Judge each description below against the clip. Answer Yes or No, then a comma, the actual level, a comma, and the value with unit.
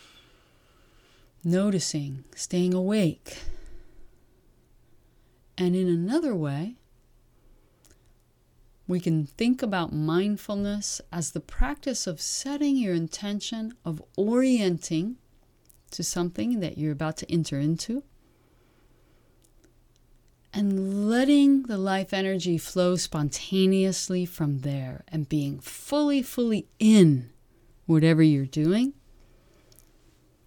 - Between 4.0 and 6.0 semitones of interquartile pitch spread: Yes, average, 5.1 semitones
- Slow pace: Yes, slow, 90 wpm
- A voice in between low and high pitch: Yes, medium, 180 Hz